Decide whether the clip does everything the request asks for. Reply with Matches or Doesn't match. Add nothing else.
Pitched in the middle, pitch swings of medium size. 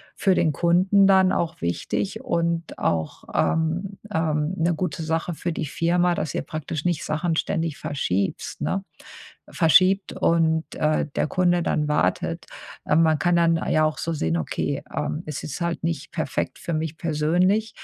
Doesn't match